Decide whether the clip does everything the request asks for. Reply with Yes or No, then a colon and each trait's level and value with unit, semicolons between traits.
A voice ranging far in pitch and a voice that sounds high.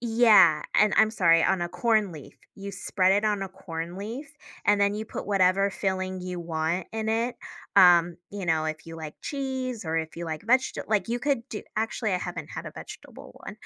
No: average, 4.3 semitones; high, 195 Hz